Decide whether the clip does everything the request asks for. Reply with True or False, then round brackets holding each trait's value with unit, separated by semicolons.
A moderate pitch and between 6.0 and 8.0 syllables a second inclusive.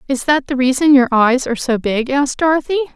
False (270 Hz; 6.3 syllables/s)